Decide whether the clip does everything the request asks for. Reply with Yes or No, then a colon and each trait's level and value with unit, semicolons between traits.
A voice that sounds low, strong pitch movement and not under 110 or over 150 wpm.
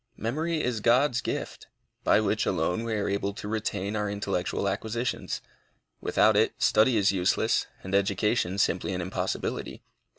No: low, 105 Hz; average, 2.8 semitones; average, 145 wpm